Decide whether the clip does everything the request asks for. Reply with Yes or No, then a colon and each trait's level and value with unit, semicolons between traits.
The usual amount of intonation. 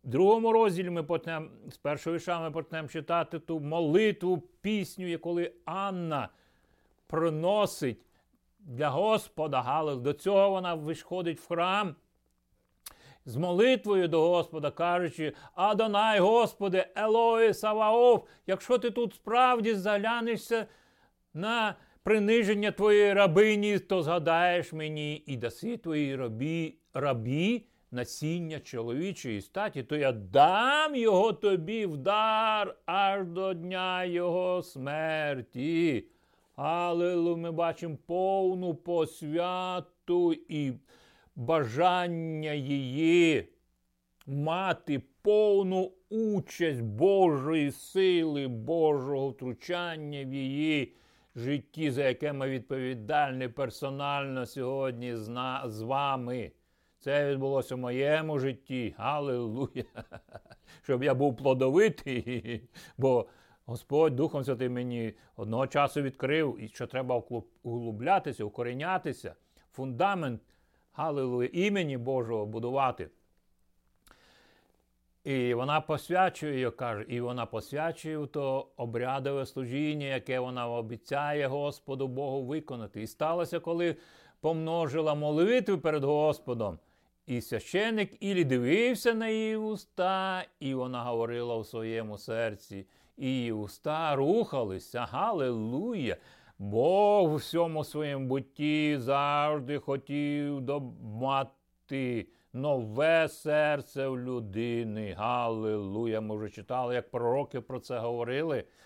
No: wide, 5.7 semitones